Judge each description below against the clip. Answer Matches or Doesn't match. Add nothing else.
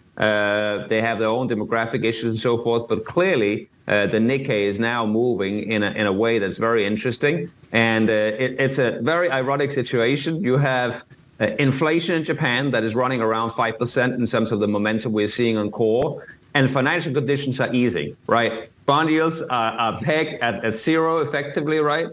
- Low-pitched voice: Matches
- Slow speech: Doesn't match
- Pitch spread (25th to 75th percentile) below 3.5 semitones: Doesn't match